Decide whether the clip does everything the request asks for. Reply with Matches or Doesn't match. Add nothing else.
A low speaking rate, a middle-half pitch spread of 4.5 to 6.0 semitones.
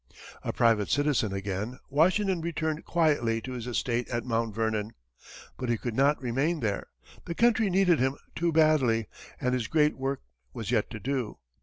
Doesn't match